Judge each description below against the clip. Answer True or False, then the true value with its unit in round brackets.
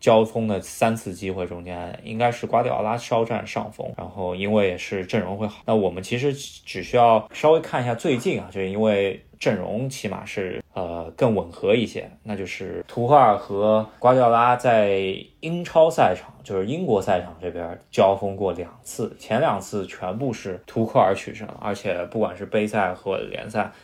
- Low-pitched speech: True (110 Hz)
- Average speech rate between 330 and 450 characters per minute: False (275 characters per minute)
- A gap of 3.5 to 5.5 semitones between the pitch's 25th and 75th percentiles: True (3.9 semitones)